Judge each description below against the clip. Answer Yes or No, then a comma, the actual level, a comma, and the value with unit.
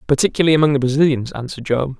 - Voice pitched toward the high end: No, medium, 140 Hz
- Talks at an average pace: Yes, average, 180 wpm